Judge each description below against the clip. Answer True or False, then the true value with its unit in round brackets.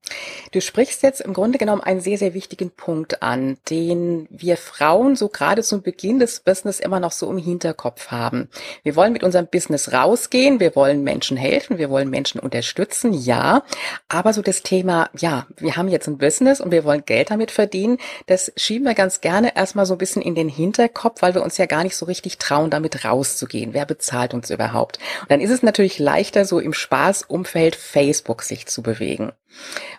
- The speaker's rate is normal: False (195 wpm)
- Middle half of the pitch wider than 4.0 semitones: True (4.9 semitones)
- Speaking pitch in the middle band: True (180 Hz)